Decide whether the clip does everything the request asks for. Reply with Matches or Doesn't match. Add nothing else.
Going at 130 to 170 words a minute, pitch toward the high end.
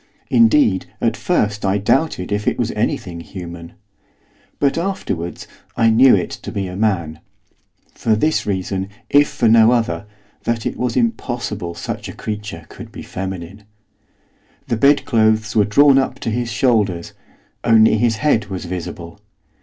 Doesn't match